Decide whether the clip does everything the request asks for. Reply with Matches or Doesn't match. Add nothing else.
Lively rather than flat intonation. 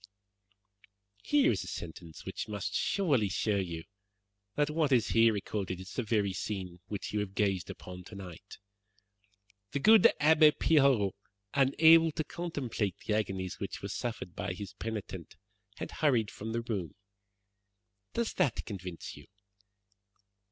Matches